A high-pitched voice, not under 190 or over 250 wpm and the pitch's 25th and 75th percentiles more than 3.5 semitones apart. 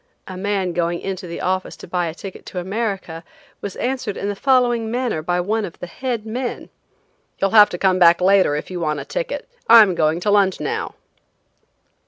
Yes: high, 195 Hz; average, 200 wpm; average, 4.1 semitones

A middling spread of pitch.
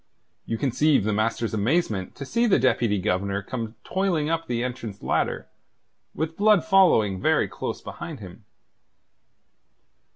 No: wide, 7.8 semitones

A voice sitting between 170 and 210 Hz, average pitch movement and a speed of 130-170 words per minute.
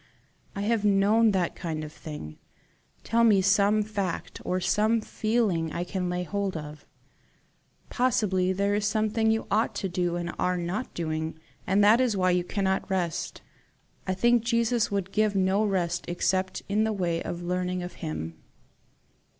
Yes: high, 190 Hz; average, 3.4 semitones; average, 165 wpm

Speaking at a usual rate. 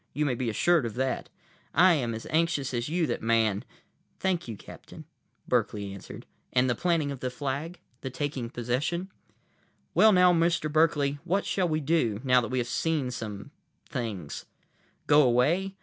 Yes: average, 165 wpm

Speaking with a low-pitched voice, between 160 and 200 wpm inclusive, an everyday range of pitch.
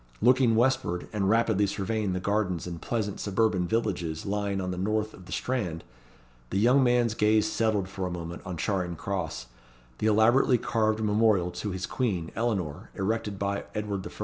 Yes: low, 105 Hz; average, 175 wpm; average, 3.3 semitones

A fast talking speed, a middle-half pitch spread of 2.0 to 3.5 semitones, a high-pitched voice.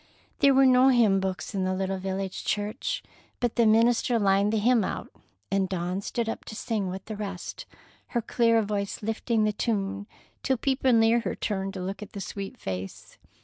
No: average, 190 wpm; average, 3.2 semitones; high, 210 Hz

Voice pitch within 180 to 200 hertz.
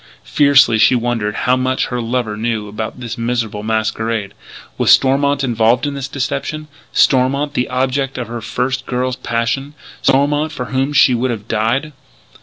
No: low, 125 Hz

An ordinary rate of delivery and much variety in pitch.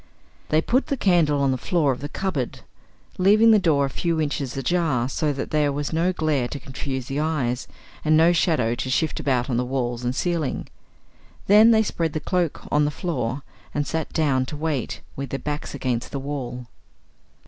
No: average, 190 wpm; average, 3.8 semitones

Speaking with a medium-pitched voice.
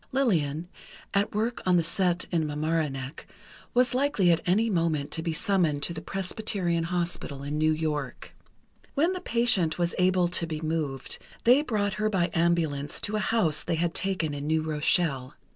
Yes: medium, 170 Hz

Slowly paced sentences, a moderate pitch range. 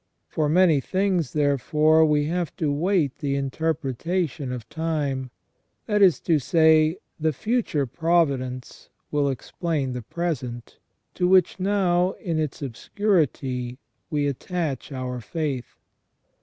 Yes: slow, 125 wpm; average, 4.3 semitones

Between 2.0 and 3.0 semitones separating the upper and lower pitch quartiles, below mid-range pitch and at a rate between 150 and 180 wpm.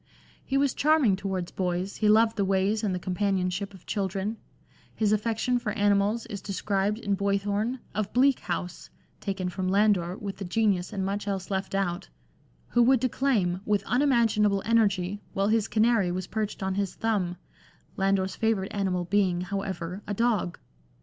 No: narrow, 2.4 semitones; high, 200 Hz; average, 170 wpm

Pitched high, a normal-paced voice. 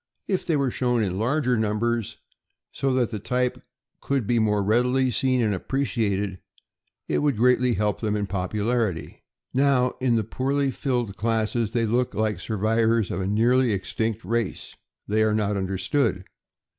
No: low, 115 Hz; average, 155 wpm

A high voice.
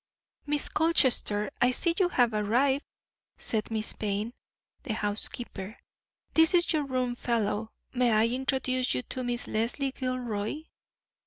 Yes: high, 245 Hz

